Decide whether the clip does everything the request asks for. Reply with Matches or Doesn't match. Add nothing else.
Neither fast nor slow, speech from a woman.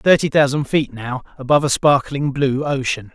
Doesn't match